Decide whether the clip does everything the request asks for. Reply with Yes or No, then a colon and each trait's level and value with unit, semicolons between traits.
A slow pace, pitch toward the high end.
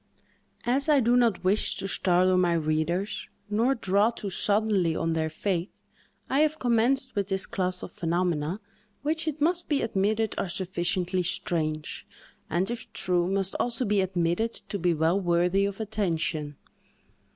No: average, 155 wpm; high, 195 Hz